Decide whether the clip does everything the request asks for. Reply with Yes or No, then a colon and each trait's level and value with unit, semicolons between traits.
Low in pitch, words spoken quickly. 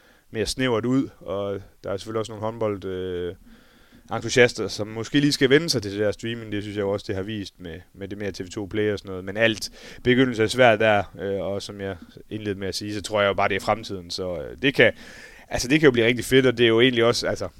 Yes: low, 105 Hz; fast, 270 wpm